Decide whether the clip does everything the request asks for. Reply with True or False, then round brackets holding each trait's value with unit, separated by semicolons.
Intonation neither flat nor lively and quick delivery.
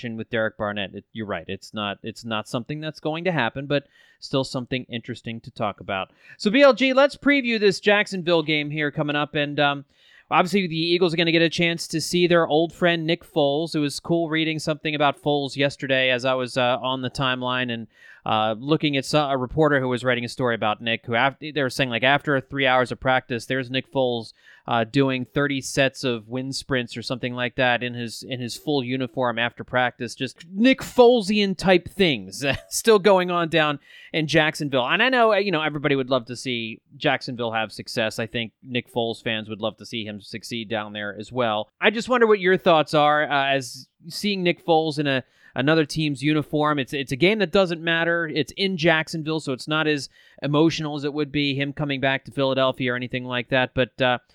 True (4.5 semitones; 220 wpm)